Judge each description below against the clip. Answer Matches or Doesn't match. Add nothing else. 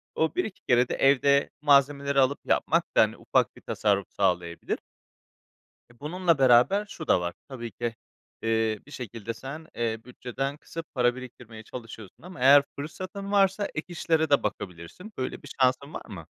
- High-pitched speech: Doesn't match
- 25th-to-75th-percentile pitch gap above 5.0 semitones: Matches